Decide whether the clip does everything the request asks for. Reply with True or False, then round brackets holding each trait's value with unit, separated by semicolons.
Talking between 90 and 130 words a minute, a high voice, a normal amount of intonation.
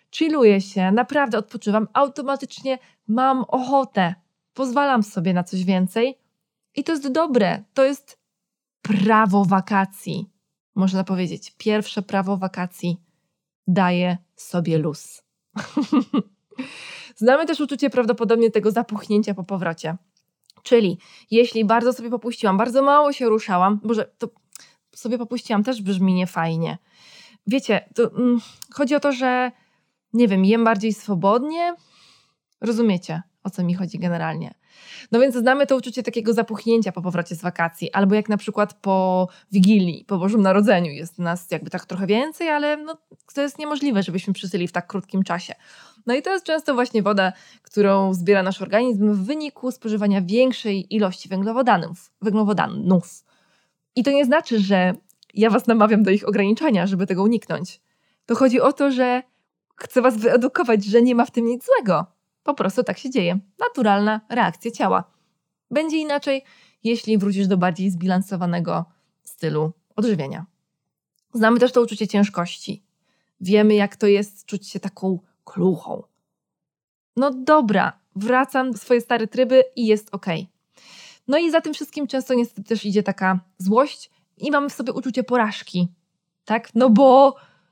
False (145 wpm; 210 Hz; 4.8 semitones)